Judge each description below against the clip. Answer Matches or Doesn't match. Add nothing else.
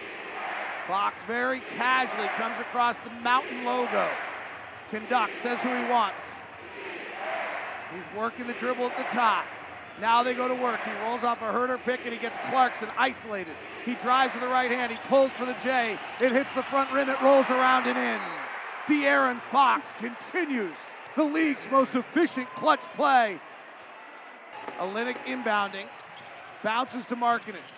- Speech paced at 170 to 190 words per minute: Doesn't match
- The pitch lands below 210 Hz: Doesn't match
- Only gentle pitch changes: Matches